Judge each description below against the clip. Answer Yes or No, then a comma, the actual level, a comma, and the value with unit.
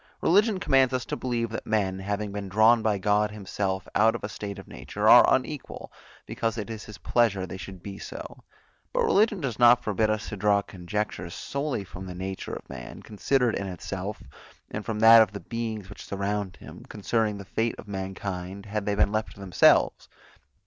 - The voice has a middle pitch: No, low, 105 Hz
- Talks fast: No, average, 195 wpm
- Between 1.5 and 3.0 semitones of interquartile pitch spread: Yes, narrow, 2.6 semitones